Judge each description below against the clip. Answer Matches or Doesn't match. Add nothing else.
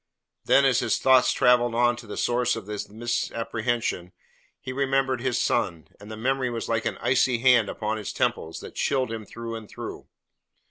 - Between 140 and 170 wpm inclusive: Doesn't match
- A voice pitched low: Matches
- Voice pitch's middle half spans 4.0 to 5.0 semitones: Doesn't match